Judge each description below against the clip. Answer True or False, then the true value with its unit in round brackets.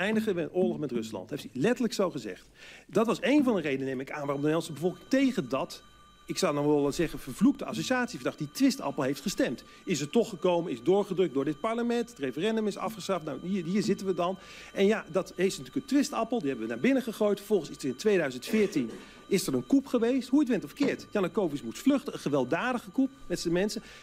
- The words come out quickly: True (230 wpm)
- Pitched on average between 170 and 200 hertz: True (190 Hz)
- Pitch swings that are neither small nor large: False (5.9 semitones)